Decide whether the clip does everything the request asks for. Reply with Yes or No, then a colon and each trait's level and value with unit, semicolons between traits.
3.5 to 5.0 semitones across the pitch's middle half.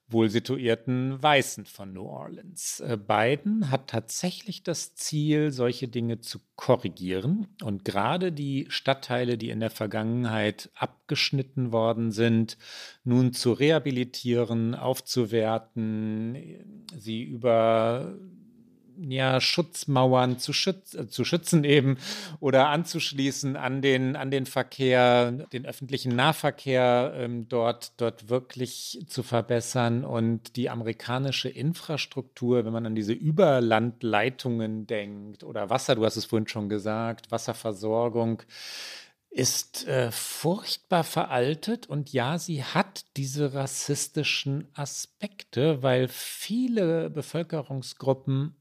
Yes: average, 4.1 semitones